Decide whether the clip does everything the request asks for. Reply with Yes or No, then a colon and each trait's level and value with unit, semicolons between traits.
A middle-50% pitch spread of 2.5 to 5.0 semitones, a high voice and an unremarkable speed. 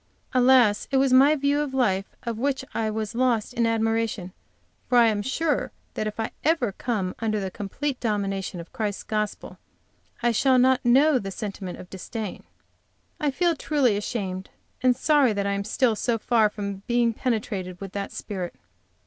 Yes: average, 4.1 semitones; high, 225 Hz; average, 175 wpm